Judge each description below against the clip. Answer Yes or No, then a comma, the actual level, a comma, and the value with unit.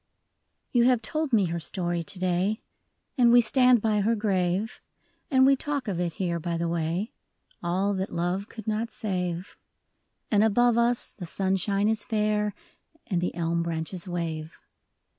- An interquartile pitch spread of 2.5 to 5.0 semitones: Yes, average, 4.2 semitones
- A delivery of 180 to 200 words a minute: No, average, 160 wpm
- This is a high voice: Yes, high, 195 Hz